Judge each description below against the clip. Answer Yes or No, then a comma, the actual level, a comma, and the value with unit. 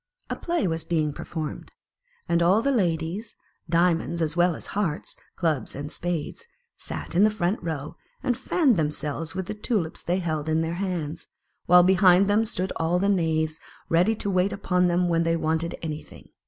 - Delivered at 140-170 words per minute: No, average, 180 wpm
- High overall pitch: No, medium, 175 Hz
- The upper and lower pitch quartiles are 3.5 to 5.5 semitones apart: No, average, 2.9 semitones